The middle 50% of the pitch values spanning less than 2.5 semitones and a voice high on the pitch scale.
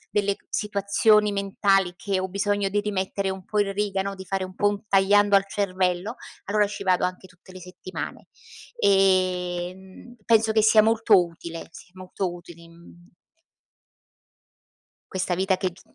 Yes: narrow, 1.8 semitones; high, 195 Hz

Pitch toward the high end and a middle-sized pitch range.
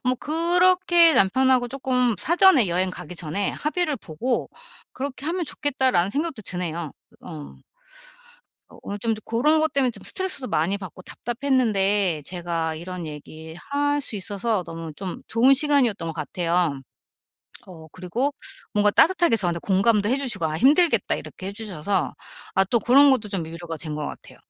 No: high, 210 Hz; wide, 7.8 semitones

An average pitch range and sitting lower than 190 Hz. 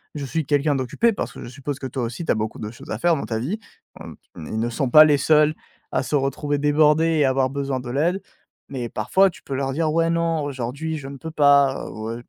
Yes: average, 3.2 semitones; medium, 140 Hz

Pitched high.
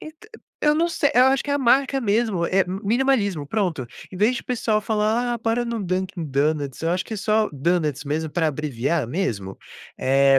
Yes: high, 195 Hz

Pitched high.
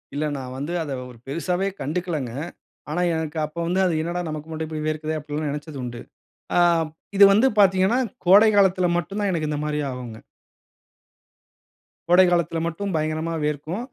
No: medium, 160 Hz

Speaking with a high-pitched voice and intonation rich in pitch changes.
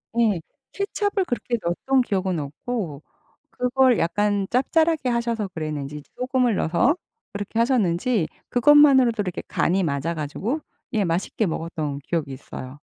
Yes: high, 205 Hz; wide, 7.2 semitones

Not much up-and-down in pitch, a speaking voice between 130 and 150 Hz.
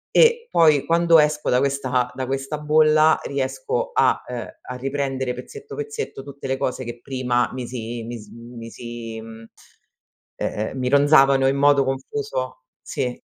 No: average, 3.7 semitones; low, 135 Hz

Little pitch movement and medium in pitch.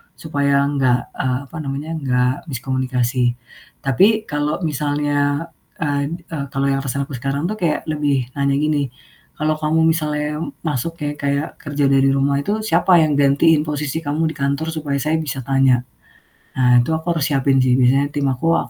Yes: narrow, 2.2 semitones; medium, 145 Hz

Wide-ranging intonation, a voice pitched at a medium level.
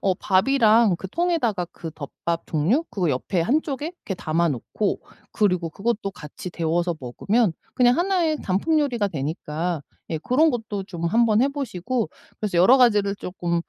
No: wide, 6.3 semitones; high, 200 Hz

